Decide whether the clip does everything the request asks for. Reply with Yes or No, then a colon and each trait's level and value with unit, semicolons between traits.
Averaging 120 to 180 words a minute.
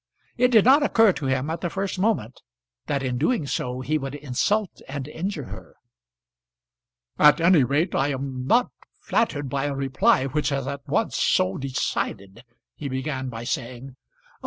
Yes: average, 170 wpm